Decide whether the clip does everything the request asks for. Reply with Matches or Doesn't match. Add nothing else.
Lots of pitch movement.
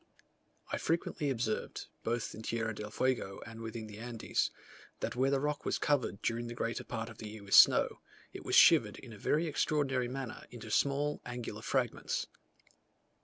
Doesn't match